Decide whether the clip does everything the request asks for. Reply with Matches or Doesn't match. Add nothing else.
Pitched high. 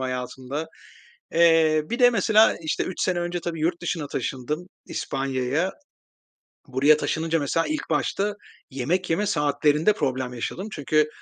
Doesn't match